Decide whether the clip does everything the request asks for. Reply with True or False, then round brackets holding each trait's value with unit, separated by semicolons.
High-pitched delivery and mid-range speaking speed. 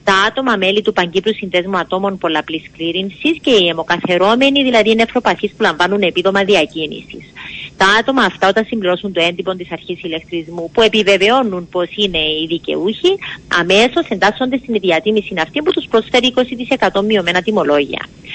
True (195 Hz; 150 wpm)